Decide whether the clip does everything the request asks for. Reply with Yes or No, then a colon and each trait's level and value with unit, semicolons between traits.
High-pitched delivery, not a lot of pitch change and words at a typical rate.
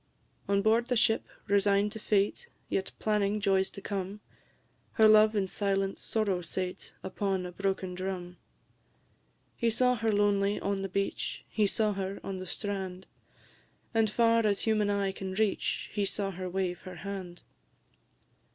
Yes: high, 200 Hz; narrow, 1.9 semitones; average, 155 wpm